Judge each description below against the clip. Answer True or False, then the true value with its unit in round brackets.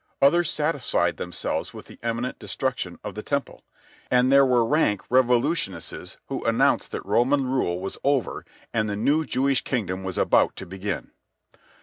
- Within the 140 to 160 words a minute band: True (150 wpm)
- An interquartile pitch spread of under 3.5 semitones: False (5.3 semitones)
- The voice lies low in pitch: True (125 Hz)